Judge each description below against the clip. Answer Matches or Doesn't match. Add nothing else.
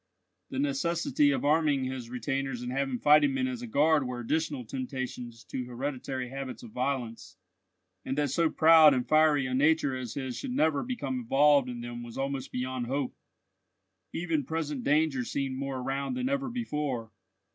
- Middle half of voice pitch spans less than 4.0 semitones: Matches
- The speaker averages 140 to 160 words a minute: Doesn't match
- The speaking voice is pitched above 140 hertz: Doesn't match